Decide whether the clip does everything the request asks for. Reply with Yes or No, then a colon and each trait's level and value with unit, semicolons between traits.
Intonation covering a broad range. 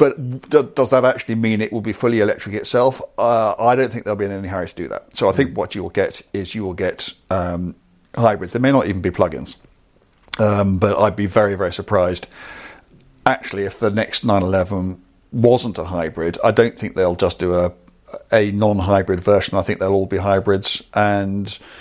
No: average, 2.8 semitones